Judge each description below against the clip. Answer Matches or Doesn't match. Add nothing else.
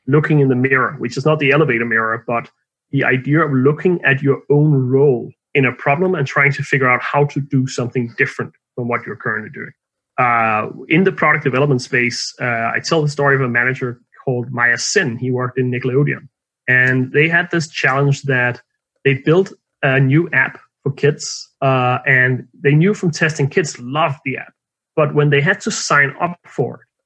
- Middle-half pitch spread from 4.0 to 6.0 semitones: Doesn't match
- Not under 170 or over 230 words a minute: Matches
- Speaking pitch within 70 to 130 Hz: Doesn't match